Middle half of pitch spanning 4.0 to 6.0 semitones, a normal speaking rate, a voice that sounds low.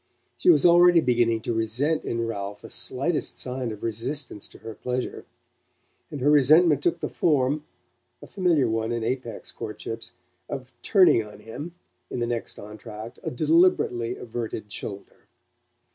Yes: average, 4.9 semitones; average, 150 wpm; low, 125 Hz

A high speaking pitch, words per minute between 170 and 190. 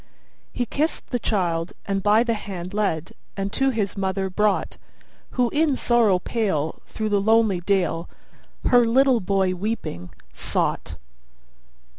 No: high, 205 Hz; slow, 135 wpm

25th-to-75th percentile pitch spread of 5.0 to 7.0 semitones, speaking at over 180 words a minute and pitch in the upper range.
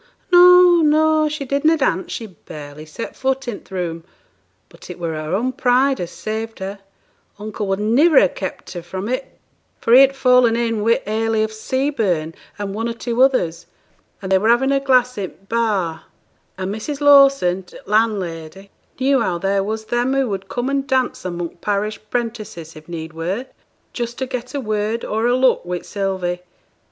Yes: wide, 5.5 semitones; average, 190 wpm; high, 220 Hz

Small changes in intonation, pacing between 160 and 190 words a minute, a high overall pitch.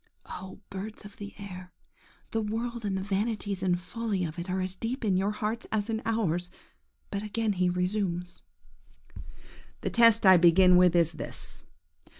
No: average, 3.2 semitones; average, 165 wpm; high, 195 Hz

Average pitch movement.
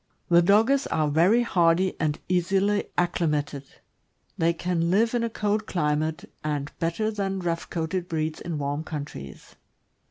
Yes: average, 4.0 semitones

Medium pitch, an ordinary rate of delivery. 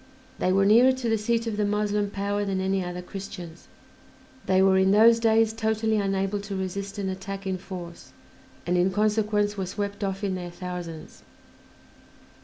No: high, 200 Hz; average, 175 wpm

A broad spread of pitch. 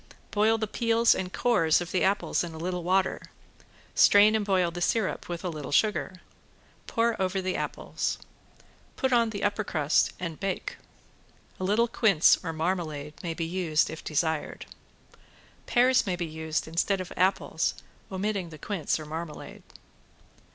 No: average, 4.0 semitones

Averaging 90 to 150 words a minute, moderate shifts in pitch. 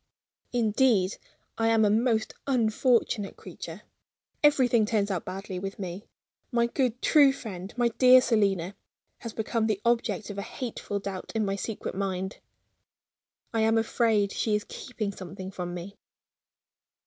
Yes: average, 145 wpm; average, 3.2 semitones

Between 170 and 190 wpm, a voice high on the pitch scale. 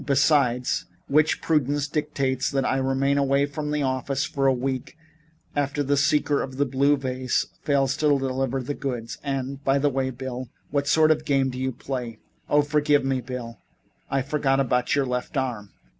No: average, 180 wpm; low, 135 Hz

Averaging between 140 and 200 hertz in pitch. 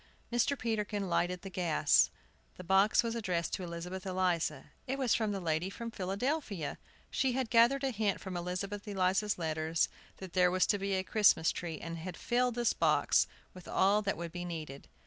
Yes: high, 190 Hz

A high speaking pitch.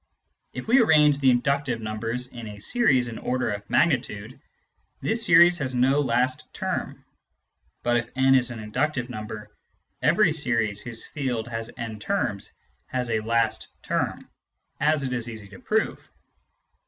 No: low, 125 Hz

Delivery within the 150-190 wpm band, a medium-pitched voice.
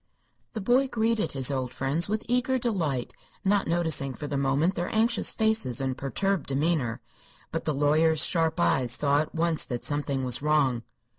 Yes: average, 170 wpm; medium, 155 Hz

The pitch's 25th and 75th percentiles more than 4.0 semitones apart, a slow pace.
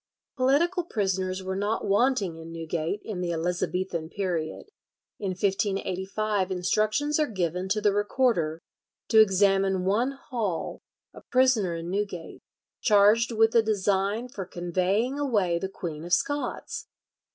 No: average, 3.7 semitones; slow, 130 wpm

